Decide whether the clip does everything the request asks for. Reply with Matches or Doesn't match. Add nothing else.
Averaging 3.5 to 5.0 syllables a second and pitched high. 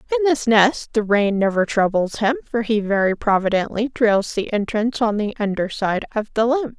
Doesn't match